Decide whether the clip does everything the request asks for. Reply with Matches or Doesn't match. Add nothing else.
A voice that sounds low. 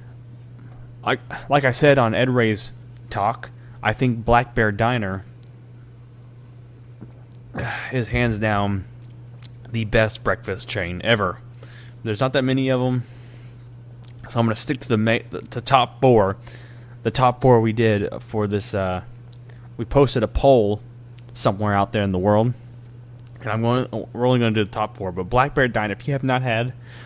Matches